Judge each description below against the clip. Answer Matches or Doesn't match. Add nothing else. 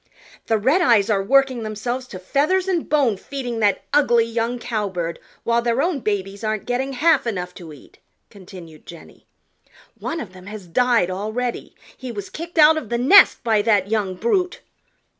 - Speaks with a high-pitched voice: Matches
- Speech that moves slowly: Doesn't match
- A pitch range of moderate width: Matches